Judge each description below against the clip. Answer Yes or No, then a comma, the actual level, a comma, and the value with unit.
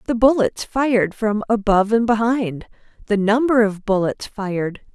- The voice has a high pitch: Yes, high, 215 Hz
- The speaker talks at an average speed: Yes, average, 145 wpm